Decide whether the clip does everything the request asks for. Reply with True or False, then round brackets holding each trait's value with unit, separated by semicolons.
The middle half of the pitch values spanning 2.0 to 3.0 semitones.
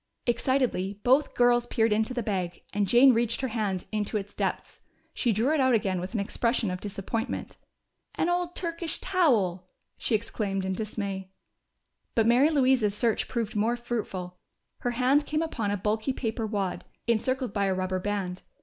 False (4.1 semitones)